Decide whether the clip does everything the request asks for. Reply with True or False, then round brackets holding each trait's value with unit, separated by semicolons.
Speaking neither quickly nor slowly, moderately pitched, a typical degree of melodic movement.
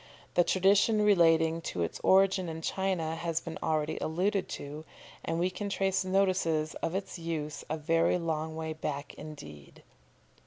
True (155 wpm; 165 Hz; 3.1 semitones)